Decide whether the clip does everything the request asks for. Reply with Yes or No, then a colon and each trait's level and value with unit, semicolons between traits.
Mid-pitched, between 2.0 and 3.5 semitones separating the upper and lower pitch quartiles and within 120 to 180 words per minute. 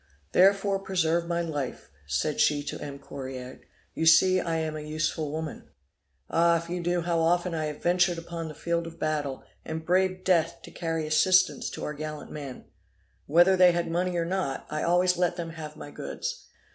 No: medium, 165 Hz; narrow, 2.5 semitones; average, 190 wpm